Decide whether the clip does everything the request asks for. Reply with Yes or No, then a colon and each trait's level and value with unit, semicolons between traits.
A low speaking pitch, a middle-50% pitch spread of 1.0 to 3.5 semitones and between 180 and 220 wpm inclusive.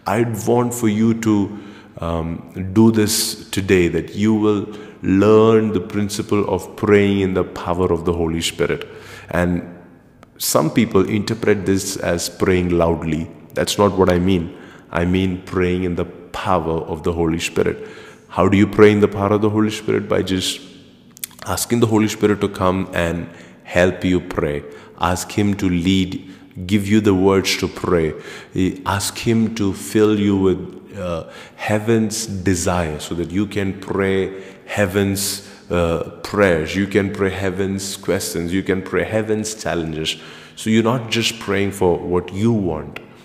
No: very low, 95 Hz; average, 3.1 semitones; average, 160 wpm